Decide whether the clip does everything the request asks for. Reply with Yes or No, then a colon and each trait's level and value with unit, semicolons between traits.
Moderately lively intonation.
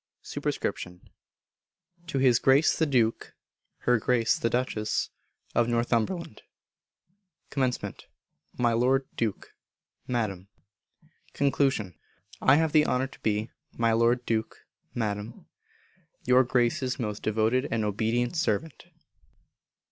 Yes: average, 3.0 semitones